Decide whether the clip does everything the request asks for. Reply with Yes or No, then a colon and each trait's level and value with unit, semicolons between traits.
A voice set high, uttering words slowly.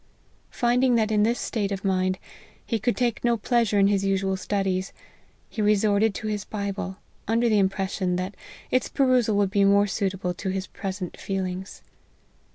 No: high, 200 Hz; average, 165 wpm